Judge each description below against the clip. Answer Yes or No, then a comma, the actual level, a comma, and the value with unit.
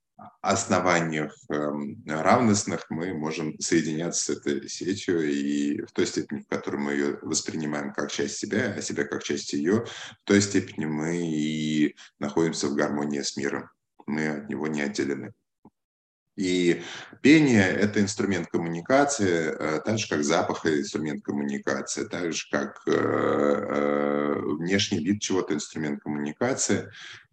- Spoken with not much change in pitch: No, average, 3.8 semitones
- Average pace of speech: No, slow, 130 wpm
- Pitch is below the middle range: Yes, very low, 75 Hz